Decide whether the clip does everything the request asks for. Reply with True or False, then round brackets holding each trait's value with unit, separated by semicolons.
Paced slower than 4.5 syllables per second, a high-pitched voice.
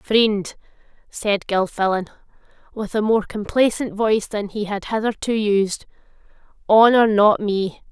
True (4.2 syllables/s; 210 Hz)